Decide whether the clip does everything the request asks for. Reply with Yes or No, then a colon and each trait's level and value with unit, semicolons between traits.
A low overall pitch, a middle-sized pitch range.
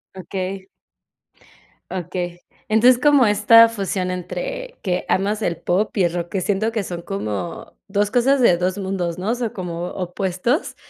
No: high, 195 Hz; average, 3.9 semitones